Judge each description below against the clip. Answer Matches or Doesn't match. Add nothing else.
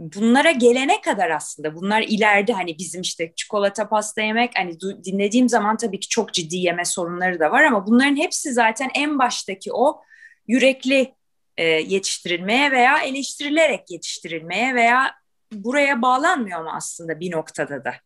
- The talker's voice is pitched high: Matches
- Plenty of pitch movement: Matches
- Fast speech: Matches